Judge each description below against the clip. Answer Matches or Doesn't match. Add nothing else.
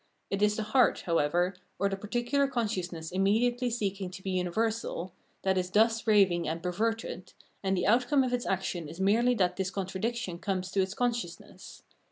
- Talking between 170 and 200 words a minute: Matches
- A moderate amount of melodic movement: Matches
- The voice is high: Matches